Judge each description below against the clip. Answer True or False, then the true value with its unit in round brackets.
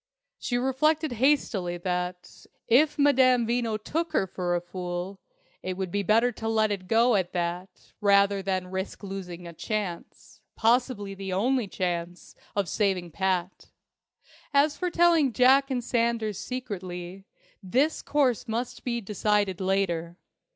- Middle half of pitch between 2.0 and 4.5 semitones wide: False (5.2 semitones)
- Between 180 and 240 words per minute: False (140 wpm)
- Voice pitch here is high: True (205 Hz)